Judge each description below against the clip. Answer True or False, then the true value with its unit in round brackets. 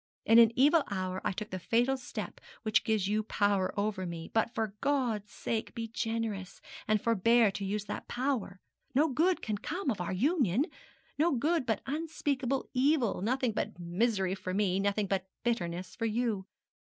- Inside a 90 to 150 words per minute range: False (180 wpm)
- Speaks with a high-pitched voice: True (220 Hz)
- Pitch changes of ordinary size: True (4.7 semitones)